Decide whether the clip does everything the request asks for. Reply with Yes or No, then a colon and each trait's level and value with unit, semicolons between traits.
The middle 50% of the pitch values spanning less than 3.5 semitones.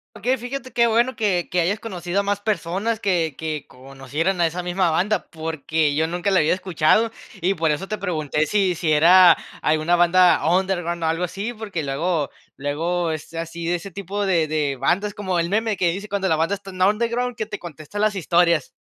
No: average, 3.8 semitones